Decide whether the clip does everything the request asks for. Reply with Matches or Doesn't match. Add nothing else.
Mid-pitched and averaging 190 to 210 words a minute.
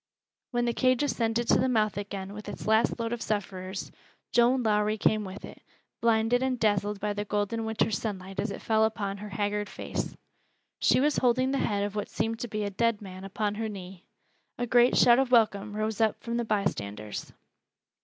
Doesn't match